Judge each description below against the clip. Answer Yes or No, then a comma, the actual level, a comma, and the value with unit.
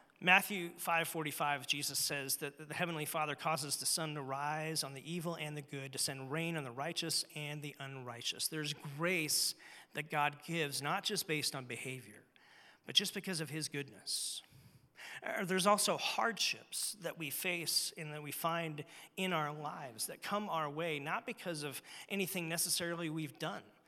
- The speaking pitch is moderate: Yes, medium, 155 Hz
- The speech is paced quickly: No, average, 170 wpm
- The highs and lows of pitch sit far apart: No, average, 3.0 semitones